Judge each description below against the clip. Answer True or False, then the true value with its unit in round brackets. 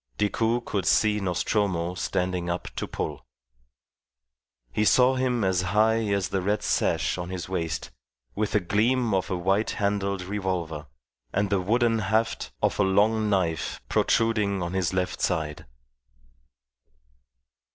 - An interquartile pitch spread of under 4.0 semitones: True (3.0 semitones)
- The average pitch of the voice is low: True (100 Hz)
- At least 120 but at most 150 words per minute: True (140 wpm)